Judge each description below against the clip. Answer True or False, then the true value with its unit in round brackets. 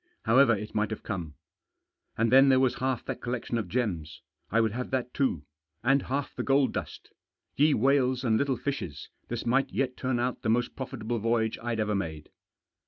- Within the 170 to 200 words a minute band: True (195 wpm)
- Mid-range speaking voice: False (120 Hz)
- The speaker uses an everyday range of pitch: True (3.2 semitones)